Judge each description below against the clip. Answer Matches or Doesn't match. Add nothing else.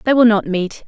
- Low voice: Doesn't match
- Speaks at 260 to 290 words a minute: Matches